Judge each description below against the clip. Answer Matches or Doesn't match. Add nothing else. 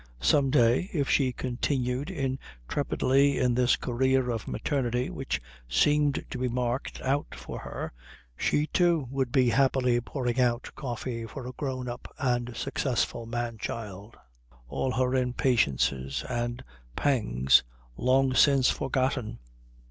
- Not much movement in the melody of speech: Matches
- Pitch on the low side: Matches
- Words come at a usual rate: Doesn't match